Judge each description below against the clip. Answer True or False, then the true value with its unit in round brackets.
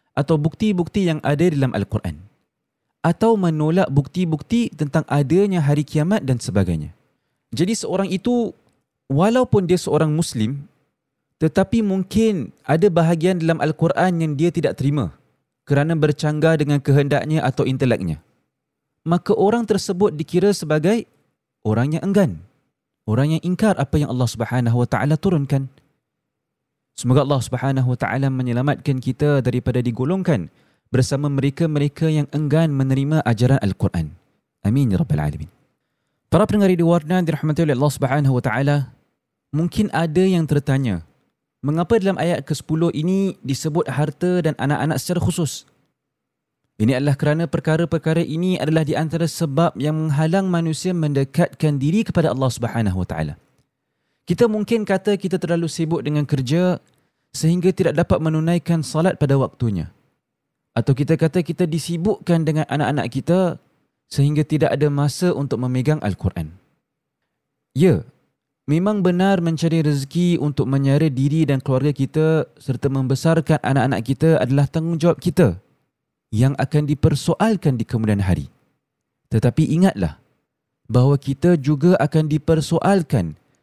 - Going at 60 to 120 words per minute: False (130 wpm)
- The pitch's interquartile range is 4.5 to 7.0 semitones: False (3.9 semitones)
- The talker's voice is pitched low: False (155 Hz)